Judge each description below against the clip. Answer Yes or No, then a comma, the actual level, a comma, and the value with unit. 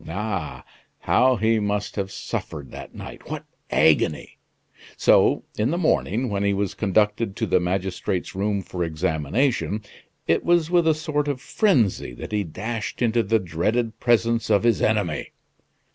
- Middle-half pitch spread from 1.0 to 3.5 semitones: No, average, 3.9 semitones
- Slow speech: No, average, 155 wpm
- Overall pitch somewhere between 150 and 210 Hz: No, low, 105 Hz